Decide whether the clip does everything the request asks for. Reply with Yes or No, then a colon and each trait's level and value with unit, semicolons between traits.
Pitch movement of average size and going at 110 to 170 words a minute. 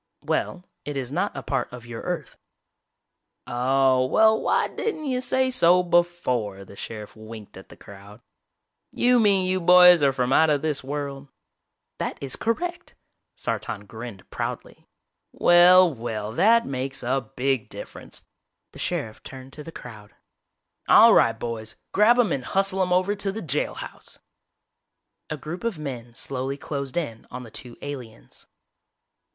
No: wide, 7.1 semitones; average, 155 wpm